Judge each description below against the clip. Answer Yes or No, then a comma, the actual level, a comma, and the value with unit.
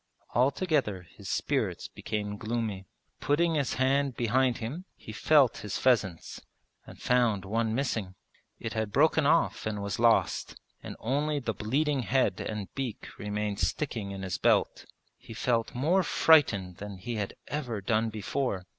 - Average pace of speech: Yes, average, 150 wpm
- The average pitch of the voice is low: Yes, low, 115 Hz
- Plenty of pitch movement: No, average, 4.8 semitones